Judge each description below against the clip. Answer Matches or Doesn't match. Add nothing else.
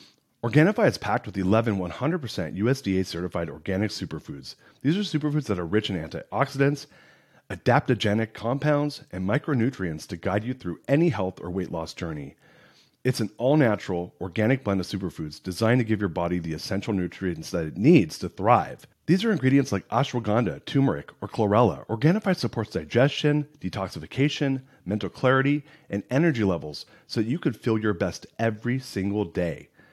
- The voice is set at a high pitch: Doesn't match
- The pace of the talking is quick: Doesn't match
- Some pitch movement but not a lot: Doesn't match